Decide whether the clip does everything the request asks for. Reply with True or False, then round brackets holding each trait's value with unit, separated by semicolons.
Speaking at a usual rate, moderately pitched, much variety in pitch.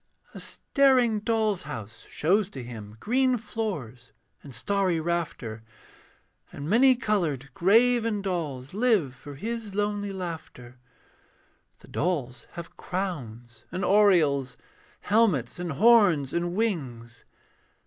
False (110 wpm; 175 Hz; 7.8 semitones)